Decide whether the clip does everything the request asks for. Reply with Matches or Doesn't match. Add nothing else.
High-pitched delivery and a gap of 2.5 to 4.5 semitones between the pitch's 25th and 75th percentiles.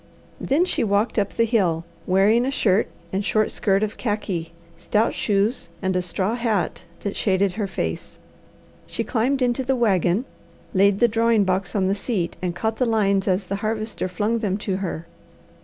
Matches